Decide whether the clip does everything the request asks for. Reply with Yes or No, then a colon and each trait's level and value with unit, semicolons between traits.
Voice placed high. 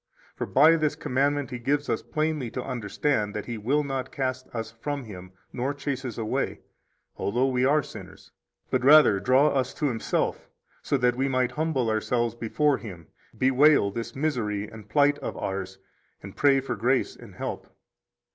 No: low, 130 Hz